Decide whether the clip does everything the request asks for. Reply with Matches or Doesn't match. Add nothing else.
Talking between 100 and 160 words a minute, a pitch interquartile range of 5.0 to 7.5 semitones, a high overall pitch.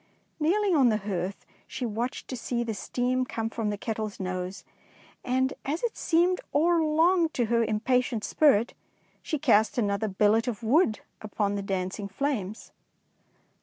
Matches